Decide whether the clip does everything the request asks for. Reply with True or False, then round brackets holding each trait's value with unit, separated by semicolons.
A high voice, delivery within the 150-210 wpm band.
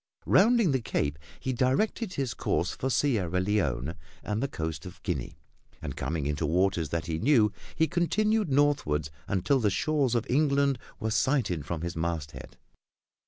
False (110 Hz; 160 wpm)